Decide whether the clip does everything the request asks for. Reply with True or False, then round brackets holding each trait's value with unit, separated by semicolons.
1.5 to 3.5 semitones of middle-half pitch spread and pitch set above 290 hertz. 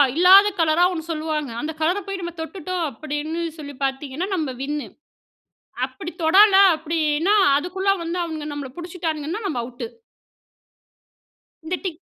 True (3.1 semitones; 320 Hz)